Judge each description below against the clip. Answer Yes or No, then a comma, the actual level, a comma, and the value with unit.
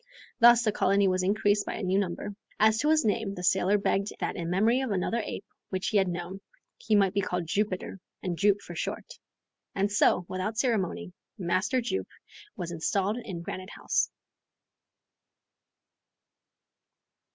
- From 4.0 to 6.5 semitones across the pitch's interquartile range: No, narrow, 2.6 semitones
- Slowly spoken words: No, average, 165 wpm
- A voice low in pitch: No, high, 200 Hz